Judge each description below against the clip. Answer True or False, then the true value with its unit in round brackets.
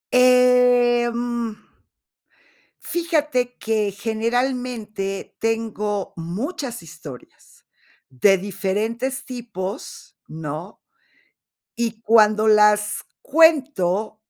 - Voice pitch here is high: True (225 Hz)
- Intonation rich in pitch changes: False (3.6 semitones)